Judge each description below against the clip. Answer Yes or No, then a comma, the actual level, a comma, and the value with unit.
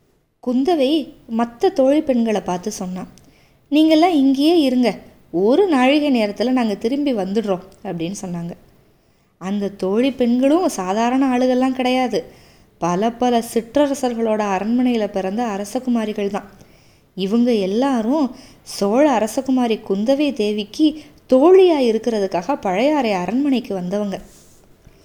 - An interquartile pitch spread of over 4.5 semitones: Yes, average, 5.1 semitones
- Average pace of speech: Yes, average, 100 wpm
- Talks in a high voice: Yes, high, 235 Hz